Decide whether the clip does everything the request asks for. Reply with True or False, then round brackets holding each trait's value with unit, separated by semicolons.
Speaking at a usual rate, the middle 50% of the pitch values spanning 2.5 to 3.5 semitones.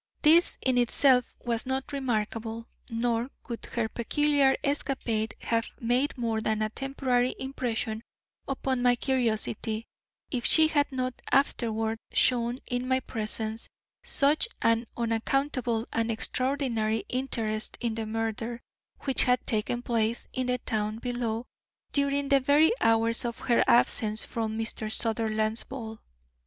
False (130 wpm; 2.8 semitones)